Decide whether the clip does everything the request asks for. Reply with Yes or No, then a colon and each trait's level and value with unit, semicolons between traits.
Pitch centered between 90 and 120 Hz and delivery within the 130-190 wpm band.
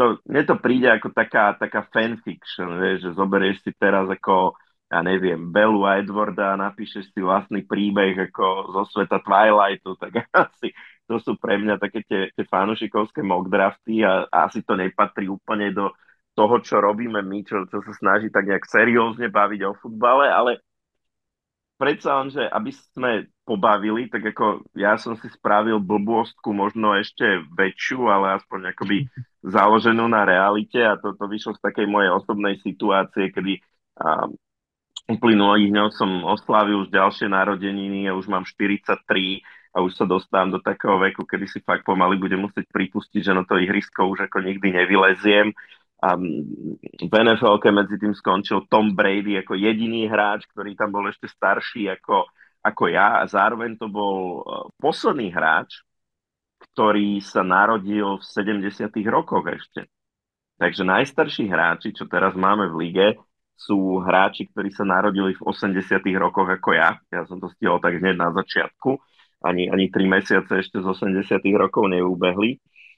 Yes: low, 100 Hz; average, 160 wpm